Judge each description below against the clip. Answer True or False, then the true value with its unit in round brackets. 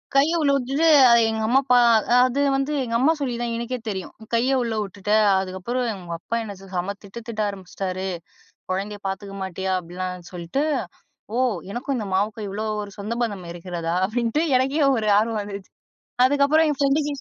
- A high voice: True (215 Hz)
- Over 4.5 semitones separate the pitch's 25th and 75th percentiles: True (5.0 semitones)